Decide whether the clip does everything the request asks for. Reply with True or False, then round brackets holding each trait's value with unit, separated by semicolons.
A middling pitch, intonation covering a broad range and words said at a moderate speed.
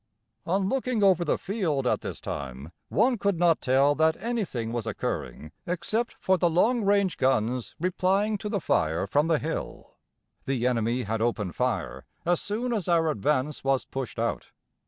True (160 Hz; 8.6 semitones; 170 wpm)